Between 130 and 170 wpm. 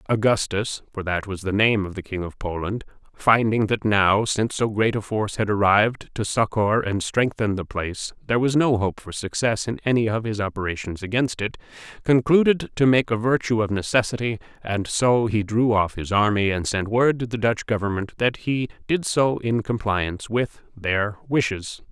No: average, 190 wpm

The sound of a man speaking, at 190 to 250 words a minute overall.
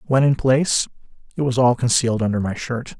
Yes: male; average, 200 wpm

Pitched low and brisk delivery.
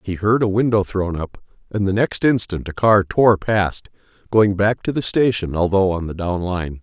Yes: low, 100 Hz; fast, 210 wpm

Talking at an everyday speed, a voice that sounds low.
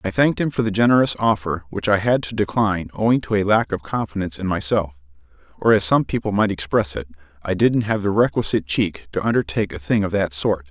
No: fast, 225 wpm; very low, 95 Hz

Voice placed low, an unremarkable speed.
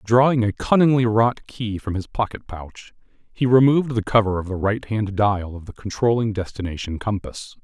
Yes: low, 110 Hz; average, 175 wpm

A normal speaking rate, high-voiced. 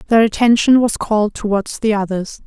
Yes: average, 170 wpm; high, 215 Hz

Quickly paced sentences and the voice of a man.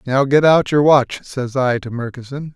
Yes: fast, 210 wpm; male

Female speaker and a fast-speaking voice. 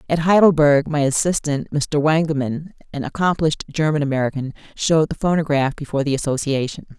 No: female; slow, 135 wpm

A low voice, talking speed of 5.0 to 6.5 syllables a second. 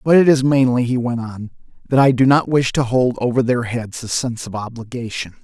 Yes: low, 125 Hz; 5.5 syllables/s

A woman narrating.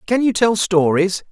No: male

